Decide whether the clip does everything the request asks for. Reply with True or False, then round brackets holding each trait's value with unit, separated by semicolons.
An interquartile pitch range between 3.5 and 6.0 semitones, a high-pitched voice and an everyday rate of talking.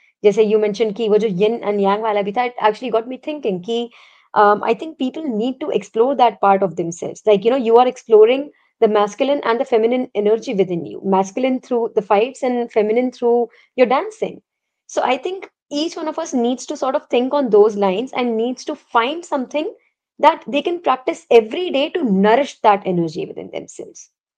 True (4.2 semitones; 235 Hz; 190 wpm)